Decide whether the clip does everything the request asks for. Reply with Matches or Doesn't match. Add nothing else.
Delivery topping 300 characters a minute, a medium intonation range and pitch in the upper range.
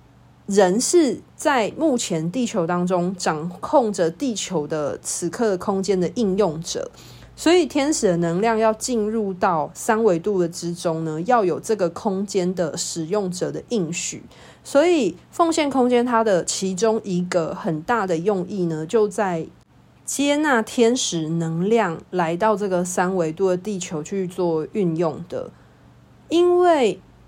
Doesn't match